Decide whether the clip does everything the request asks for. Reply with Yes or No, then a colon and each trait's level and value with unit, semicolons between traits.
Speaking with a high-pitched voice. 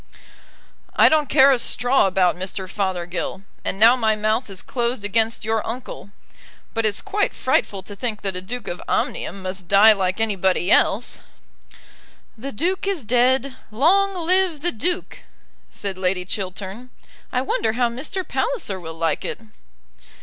Yes: high, 220 Hz